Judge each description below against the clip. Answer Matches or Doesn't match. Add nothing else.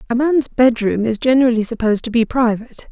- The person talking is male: Doesn't match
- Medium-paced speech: Matches